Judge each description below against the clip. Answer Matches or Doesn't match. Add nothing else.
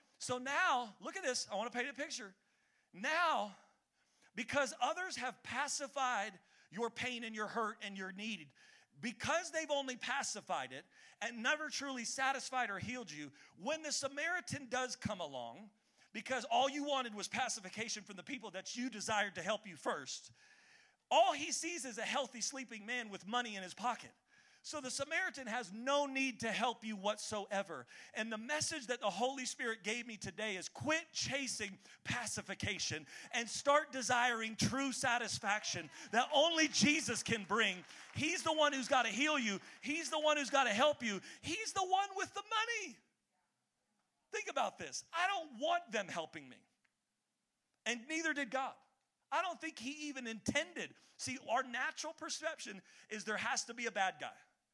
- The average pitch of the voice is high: Matches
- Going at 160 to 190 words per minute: Matches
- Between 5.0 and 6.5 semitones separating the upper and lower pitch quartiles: Matches